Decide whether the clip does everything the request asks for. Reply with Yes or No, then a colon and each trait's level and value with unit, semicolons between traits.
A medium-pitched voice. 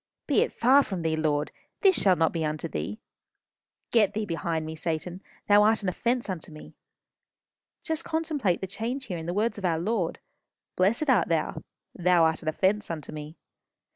Yes: medium, 180 Hz